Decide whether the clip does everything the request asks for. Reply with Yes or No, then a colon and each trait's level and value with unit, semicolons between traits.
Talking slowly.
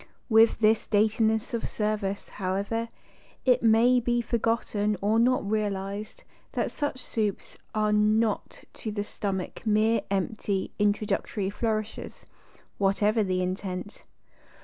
Yes: slow, 115 wpm